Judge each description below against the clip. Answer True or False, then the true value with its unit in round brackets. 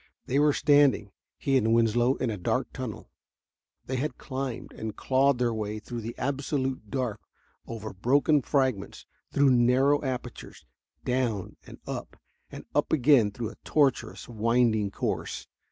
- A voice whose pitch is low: True (125 Hz)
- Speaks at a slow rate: False (145 wpm)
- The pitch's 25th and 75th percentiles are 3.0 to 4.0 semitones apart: True (3.5 semitones)